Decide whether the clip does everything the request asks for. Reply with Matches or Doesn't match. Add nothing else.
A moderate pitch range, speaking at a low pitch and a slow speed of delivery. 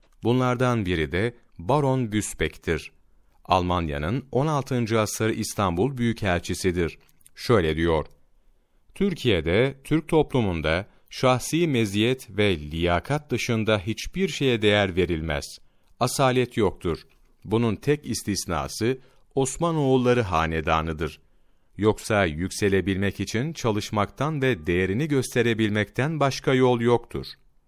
Doesn't match